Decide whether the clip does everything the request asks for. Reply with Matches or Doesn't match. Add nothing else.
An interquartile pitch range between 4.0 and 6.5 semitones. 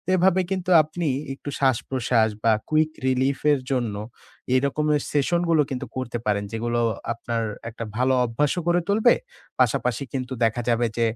Matches